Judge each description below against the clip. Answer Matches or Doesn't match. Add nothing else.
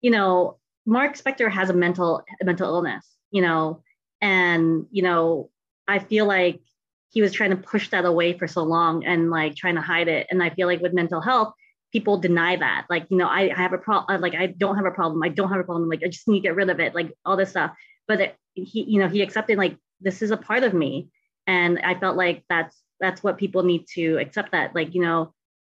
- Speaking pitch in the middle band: Matches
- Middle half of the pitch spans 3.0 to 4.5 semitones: Doesn't match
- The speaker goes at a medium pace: Doesn't match